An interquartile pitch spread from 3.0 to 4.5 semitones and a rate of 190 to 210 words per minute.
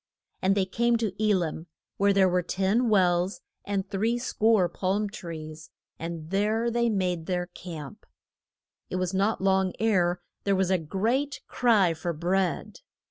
No: average, 3.3 semitones; average, 150 wpm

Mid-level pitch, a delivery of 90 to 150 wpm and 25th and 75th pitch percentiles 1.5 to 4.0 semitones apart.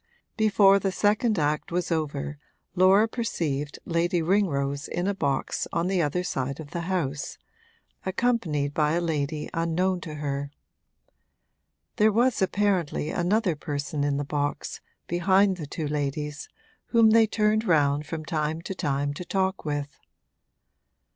No: medium, 165 Hz; average, 140 wpm; average, 4.7 semitones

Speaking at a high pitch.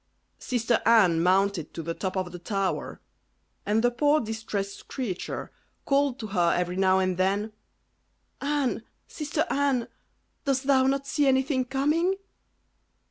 Yes: high, 230 Hz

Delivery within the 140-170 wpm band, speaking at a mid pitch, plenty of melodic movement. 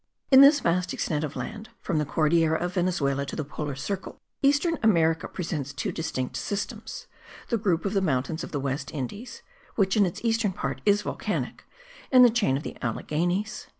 No: average, 185 wpm; medium, 175 Hz; wide, 5.8 semitones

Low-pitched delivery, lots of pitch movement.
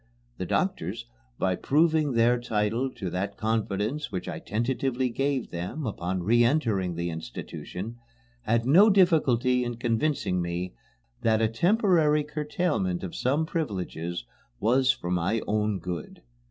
Yes: low, 115 Hz; wide, 7.0 semitones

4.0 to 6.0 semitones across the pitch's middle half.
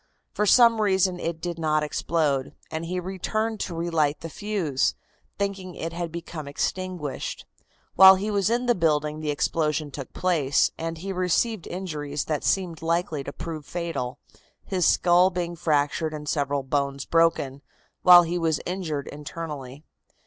No: average, 3.5 semitones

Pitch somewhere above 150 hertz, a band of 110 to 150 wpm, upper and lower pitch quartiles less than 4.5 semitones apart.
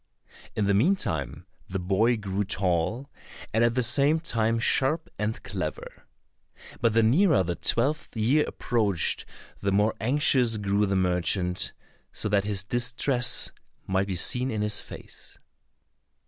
No: low, 110 Hz; average, 140 wpm; average, 4.1 semitones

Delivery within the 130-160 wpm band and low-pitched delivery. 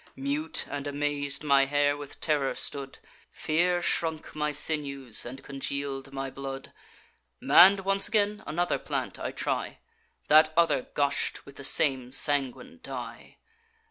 No: slow, 135 wpm; medium, 145 Hz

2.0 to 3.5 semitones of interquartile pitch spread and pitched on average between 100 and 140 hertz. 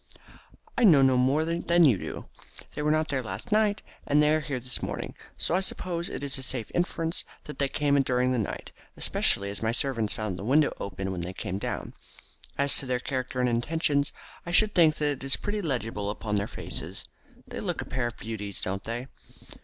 No: wide, 5.5 semitones; low, 135 Hz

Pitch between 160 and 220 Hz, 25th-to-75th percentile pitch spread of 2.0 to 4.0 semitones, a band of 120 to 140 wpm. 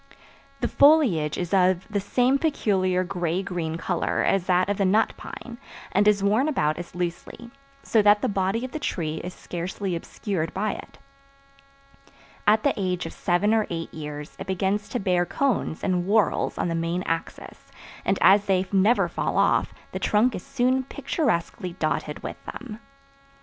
No: high, 190 Hz; average, 3.5 semitones; average, 170 wpm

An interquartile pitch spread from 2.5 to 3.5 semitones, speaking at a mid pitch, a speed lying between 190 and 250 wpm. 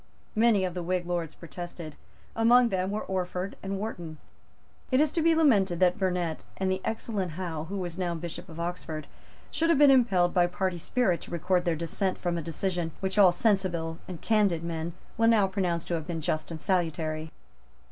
Yes: average, 2.8 semitones; medium, 180 Hz; average, 195 wpm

